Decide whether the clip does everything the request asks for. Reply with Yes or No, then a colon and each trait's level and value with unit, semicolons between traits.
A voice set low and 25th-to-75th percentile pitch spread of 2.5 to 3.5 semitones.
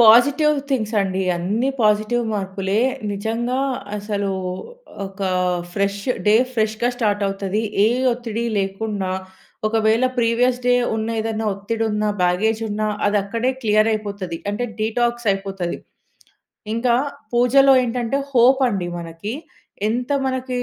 No: high, 220 Hz; average, 3.1 semitones